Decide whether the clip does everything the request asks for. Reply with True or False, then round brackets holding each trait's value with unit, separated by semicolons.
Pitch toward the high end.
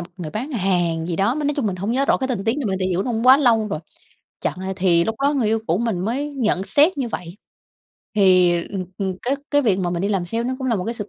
True (210 Hz)